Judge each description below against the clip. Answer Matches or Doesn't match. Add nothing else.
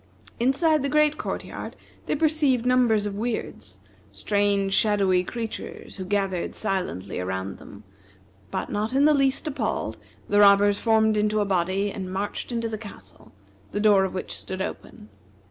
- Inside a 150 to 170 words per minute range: Matches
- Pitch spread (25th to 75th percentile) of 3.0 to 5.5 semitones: Matches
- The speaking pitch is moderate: Doesn't match